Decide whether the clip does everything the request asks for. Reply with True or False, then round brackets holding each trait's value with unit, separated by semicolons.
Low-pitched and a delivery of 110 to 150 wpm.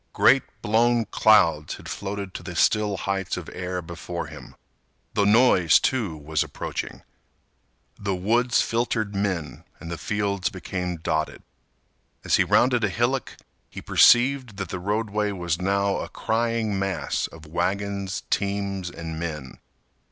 True (100 Hz; 140 wpm)